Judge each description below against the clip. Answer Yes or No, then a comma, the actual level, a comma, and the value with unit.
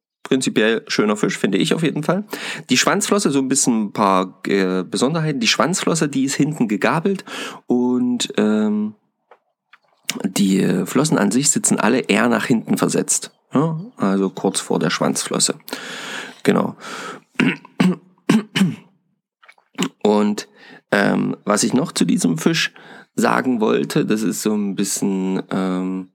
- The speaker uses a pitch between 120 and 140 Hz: Yes, low, 135 Hz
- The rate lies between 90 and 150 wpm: Yes, average, 130 wpm